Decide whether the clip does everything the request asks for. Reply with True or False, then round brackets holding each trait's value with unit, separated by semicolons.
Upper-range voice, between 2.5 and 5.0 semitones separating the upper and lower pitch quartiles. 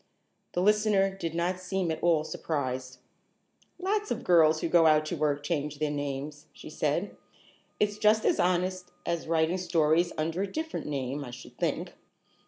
False (165 Hz; 3.7 semitones)